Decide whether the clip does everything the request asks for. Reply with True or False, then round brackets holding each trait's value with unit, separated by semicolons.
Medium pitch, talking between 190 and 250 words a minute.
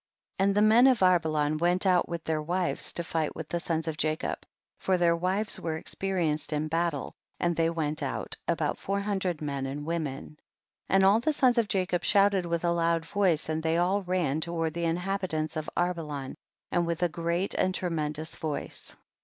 True (170 Hz; 200 wpm)